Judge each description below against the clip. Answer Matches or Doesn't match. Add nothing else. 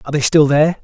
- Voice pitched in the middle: Matches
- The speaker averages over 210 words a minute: Matches